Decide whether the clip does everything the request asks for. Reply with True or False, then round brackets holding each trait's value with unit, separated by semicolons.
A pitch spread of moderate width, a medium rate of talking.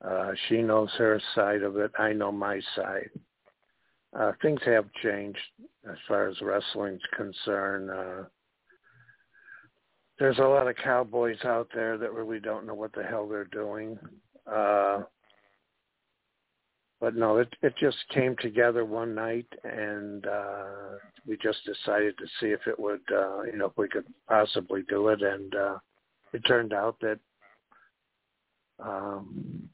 False (2.0 semitones; 150 wpm)